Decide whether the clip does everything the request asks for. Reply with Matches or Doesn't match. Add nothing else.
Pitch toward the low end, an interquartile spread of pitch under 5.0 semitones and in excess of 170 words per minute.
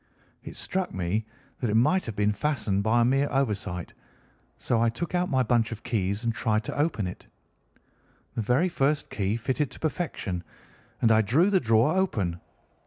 Doesn't match